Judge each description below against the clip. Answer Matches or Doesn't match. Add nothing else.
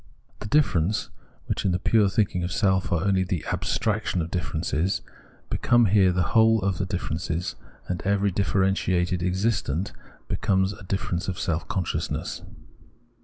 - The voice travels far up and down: Doesn't match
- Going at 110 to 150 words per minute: Matches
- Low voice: Matches